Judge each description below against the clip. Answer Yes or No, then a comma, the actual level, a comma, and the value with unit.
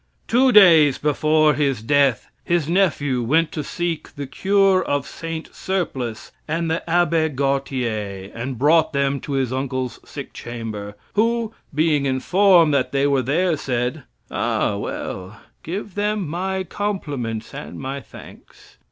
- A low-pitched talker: No, medium, 145 Hz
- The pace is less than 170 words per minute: Yes, average, 140 wpm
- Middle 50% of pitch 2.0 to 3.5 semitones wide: No, average, 4.8 semitones